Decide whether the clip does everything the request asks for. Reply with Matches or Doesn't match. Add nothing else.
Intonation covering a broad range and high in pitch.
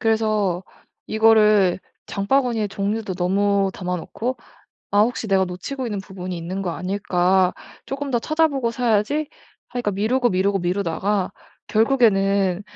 Doesn't match